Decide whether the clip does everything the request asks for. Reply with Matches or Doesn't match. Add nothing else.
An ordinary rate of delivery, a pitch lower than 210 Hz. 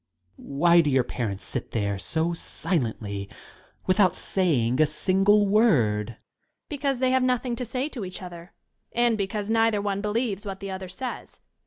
Matches